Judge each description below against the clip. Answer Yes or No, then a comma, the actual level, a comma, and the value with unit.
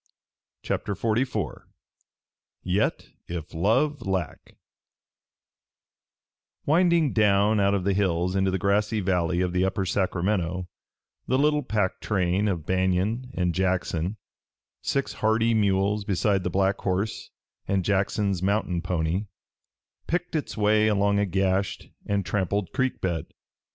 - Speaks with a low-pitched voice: Yes, low, 100 Hz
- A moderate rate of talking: No, slow, 125 wpm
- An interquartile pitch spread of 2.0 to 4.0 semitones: Yes, narrow, 2.6 semitones